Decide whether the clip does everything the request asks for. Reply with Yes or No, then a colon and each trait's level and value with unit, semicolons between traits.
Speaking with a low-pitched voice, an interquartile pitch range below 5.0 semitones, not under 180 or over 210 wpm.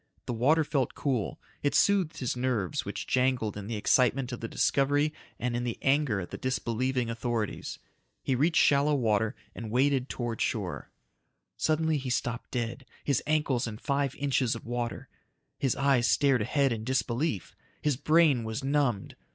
No: low, 130 Hz; average, 3.3 semitones; average, 165 wpm